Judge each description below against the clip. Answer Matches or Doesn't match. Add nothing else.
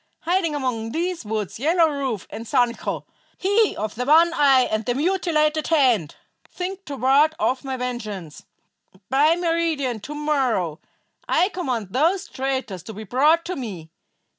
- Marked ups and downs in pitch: Matches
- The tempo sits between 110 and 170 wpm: Matches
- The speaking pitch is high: Matches